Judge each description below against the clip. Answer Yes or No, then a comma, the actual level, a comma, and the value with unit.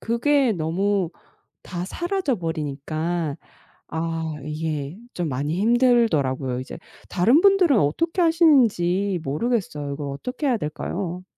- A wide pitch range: Yes, wide, 8.0 semitones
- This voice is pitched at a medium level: Yes, medium, 175 Hz